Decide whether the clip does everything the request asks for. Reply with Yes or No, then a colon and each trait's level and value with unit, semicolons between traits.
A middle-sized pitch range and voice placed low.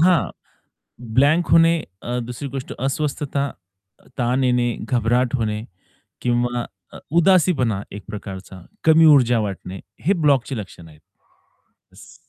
Yes: average, 4.3 semitones; low, 125 Hz